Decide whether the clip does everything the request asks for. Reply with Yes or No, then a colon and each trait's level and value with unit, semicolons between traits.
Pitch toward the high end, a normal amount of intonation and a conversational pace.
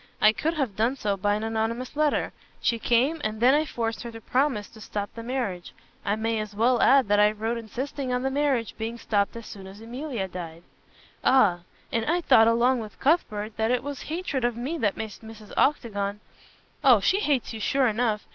No: high, 230 Hz; average, 3.7 semitones; fast, 215 wpm